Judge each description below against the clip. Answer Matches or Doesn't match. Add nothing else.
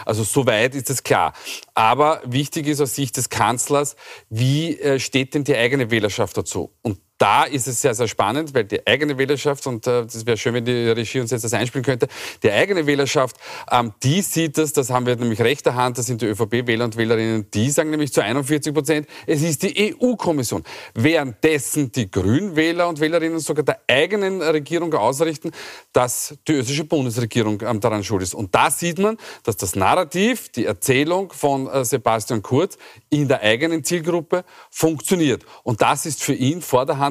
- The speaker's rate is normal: Matches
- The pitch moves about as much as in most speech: Matches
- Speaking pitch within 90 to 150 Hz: Matches